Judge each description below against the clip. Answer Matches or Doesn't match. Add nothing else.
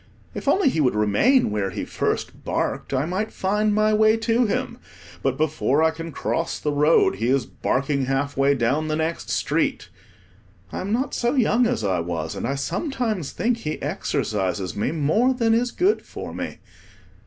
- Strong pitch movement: Matches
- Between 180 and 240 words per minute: Matches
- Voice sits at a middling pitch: Matches